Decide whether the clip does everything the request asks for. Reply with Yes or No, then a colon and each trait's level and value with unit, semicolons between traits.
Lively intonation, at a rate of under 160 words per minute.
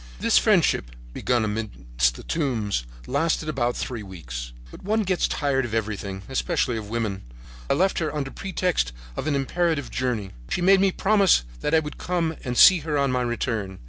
No: wide, 7.7 semitones; average, 180 wpm